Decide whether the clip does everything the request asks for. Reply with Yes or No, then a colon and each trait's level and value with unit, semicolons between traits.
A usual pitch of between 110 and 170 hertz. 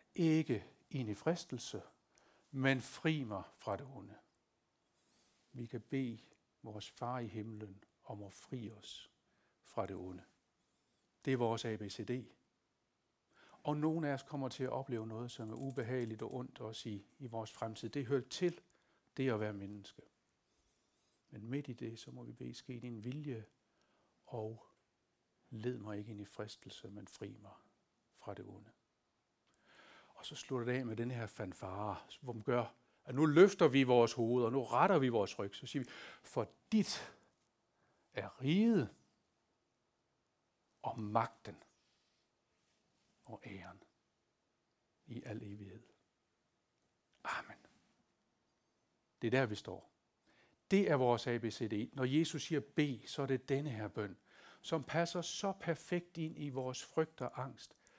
Yes: low, 125 Hz